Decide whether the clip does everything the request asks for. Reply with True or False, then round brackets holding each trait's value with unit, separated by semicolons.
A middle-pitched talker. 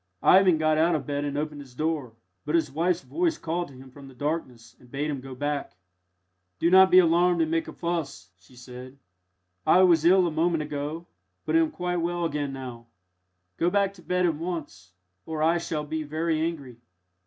True (155 Hz)